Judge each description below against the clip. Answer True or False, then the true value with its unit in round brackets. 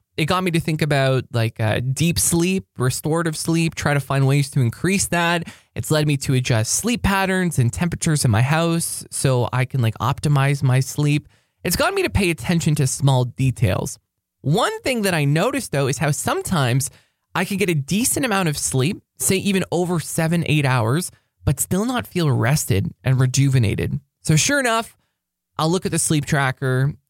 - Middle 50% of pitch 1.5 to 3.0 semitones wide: False (4.9 semitones)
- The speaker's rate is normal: True (190 wpm)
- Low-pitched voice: False (150 Hz)